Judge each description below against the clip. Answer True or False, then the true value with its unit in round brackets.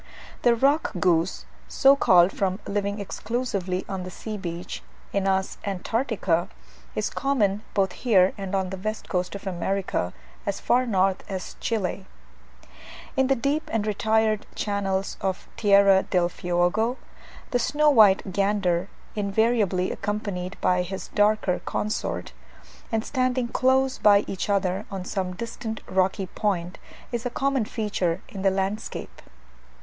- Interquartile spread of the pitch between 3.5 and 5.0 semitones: False (3.0 semitones)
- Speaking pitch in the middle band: False (200 Hz)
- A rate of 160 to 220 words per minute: False (135 wpm)